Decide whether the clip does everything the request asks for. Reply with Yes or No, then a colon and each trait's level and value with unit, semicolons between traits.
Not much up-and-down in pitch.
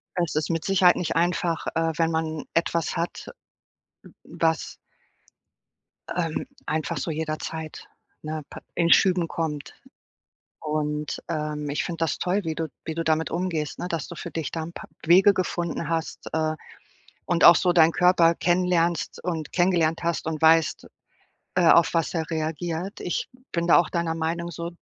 Yes: narrow, 1.5 semitones